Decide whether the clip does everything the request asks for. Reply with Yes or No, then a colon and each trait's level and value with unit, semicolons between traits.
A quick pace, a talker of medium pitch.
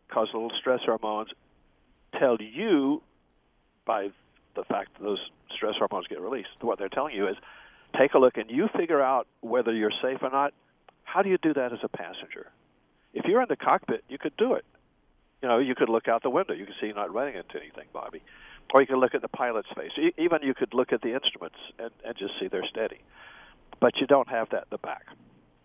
No: fast, 220 wpm; low, 110 Hz